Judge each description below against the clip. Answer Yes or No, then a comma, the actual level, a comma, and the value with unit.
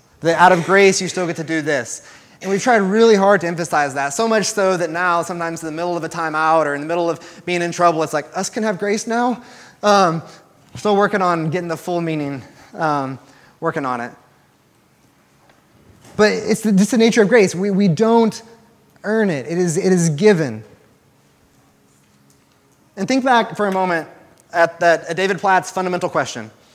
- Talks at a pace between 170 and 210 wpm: Yes, average, 195 wpm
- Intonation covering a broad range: No, average, 4.2 semitones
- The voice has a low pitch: No, medium, 175 Hz